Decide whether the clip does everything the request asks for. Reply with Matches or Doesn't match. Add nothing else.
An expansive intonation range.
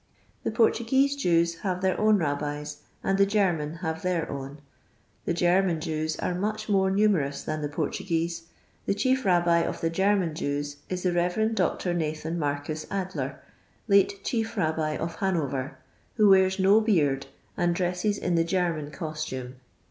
Doesn't match